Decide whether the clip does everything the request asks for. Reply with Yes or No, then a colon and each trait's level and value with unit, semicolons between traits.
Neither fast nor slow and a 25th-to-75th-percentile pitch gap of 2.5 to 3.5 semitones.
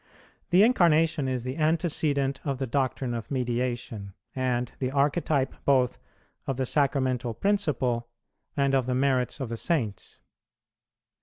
No: slow, 130 wpm; average, 2.8 semitones